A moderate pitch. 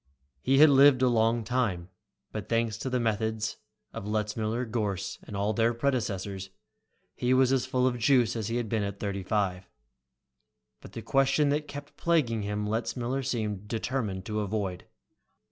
No: low, 115 Hz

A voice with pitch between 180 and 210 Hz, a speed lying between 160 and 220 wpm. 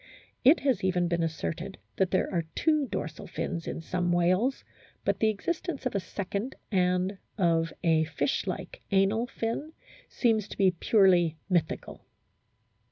No: medium, 185 Hz; average, 150 wpm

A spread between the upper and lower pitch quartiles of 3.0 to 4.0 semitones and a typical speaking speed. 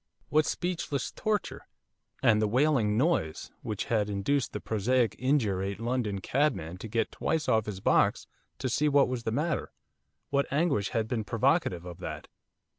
No: wide, 5.4 semitones; average, 160 wpm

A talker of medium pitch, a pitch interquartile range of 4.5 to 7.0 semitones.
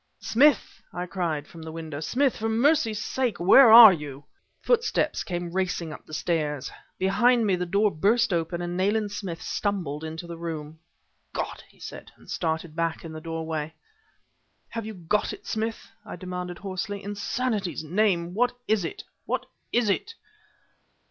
Yes: medium, 180 Hz; average, 5.0 semitones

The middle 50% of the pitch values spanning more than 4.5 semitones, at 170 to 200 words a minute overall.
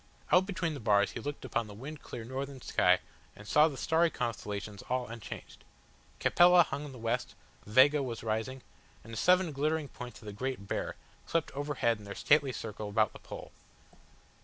Yes: average, 5.1 semitones; average, 185 wpm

